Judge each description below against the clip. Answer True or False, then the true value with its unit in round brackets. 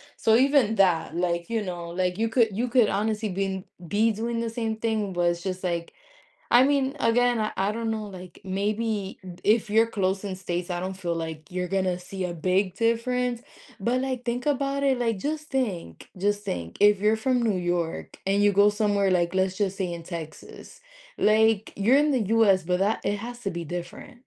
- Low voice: False (205 Hz)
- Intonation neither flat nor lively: True (3.9 semitones)